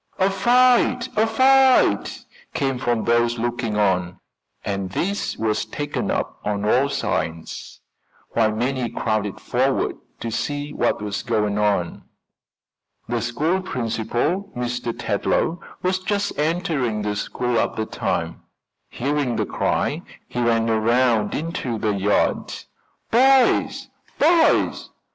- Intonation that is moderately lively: No, wide, 8.1 semitones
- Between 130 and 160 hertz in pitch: No, low, 120 Hz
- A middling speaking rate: No, slow, 120 wpm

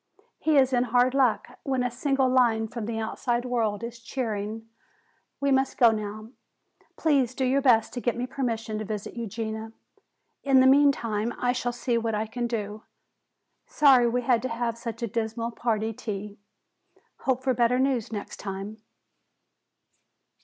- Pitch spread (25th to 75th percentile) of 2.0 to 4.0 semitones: Yes, narrow, 2.6 semitones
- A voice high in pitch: Yes, high, 235 Hz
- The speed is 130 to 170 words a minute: Yes, average, 165 wpm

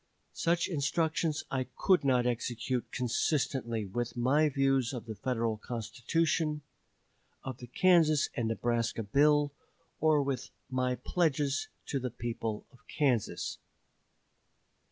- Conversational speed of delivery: No, slow, 115 wpm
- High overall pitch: No, low, 130 Hz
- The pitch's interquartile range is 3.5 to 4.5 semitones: Yes, average, 3.9 semitones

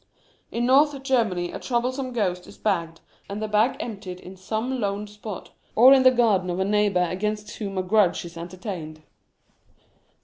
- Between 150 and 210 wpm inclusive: Yes, average, 170 wpm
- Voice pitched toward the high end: Yes, high, 210 Hz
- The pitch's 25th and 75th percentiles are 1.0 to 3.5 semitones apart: No, average, 4.5 semitones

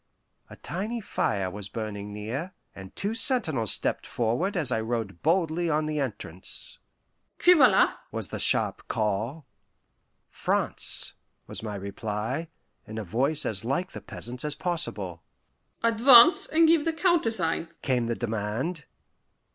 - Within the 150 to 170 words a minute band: No, average, 140 wpm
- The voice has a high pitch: No, low, 130 Hz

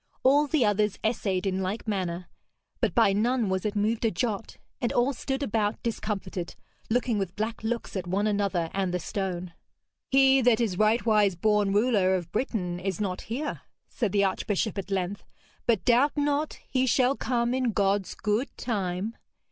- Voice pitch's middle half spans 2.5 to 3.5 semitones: No, average, 3.9 semitones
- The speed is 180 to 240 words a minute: No, average, 170 wpm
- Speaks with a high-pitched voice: Yes, high, 210 Hz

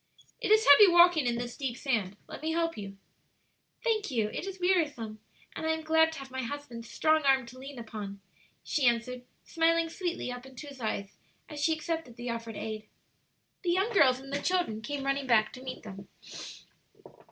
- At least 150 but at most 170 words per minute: No, average, 195 wpm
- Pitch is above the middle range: Yes, very high, 270 Hz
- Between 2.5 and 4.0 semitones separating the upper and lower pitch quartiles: No, wide, 5.5 semitones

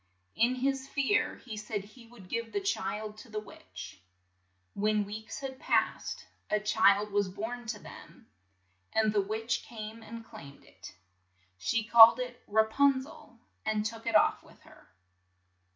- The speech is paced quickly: No, average, 170 wpm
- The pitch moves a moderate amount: No, narrow, 2.1 semitones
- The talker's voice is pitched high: Yes, high, 220 Hz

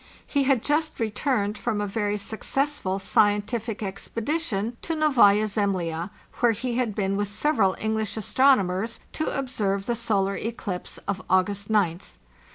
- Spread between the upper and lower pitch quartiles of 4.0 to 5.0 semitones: No, average, 3.5 semitones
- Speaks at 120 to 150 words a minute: Yes, average, 140 wpm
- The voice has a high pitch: Yes, high, 215 Hz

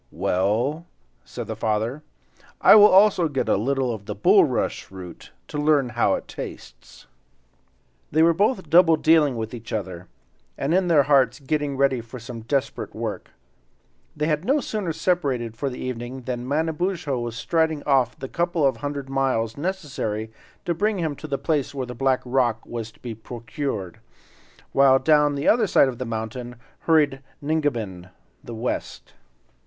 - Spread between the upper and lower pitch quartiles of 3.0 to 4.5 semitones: No, average, 5.0 semitones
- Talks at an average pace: Yes, average, 165 wpm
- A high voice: No, low, 135 Hz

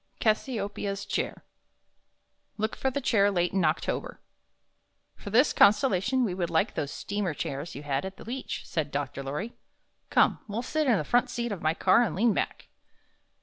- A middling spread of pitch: No, wide, 6.1 semitones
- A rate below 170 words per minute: No, average, 175 wpm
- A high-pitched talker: Yes, high, 200 Hz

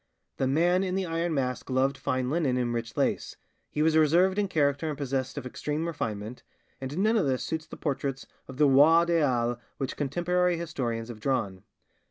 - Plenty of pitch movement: No, average, 4.6 semitones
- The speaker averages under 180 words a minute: No, average, 195 wpm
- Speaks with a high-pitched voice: No, medium, 140 Hz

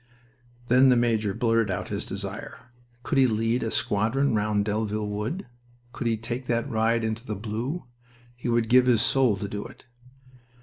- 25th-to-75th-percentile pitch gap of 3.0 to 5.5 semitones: No, narrow, 2.5 semitones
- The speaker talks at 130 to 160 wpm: No, average, 175 wpm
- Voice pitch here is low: Yes, low, 115 Hz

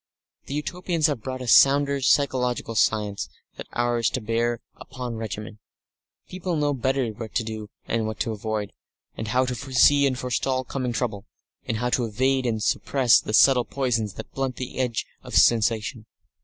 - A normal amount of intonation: Yes, average, 3.2 semitones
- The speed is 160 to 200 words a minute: Yes, average, 170 wpm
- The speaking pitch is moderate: No, low, 120 Hz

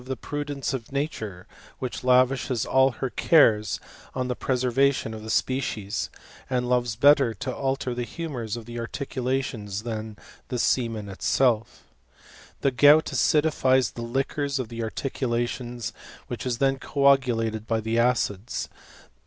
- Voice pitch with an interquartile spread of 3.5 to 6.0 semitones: No, average, 2.9 semitones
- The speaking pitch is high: No, low, 125 Hz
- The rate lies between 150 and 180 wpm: No, slow, 135 wpm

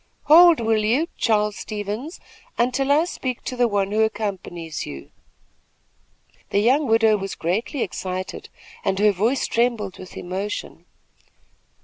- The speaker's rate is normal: No, slow, 130 wpm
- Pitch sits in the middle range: No, high, 215 Hz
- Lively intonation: No, average, 4.1 semitones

